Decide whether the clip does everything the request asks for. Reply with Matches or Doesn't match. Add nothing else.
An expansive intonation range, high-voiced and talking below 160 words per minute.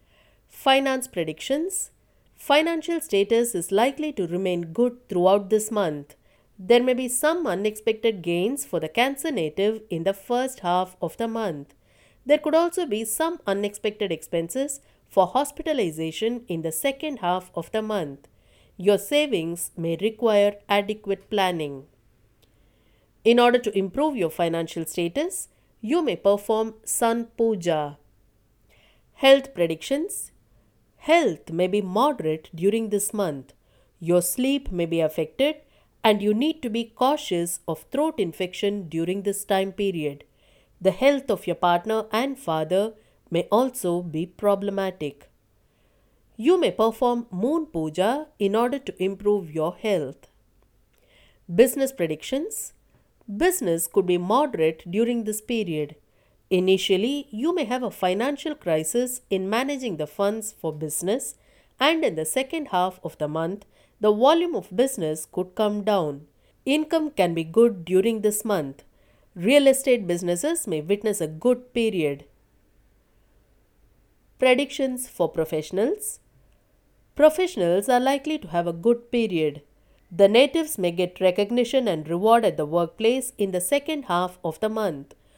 Matches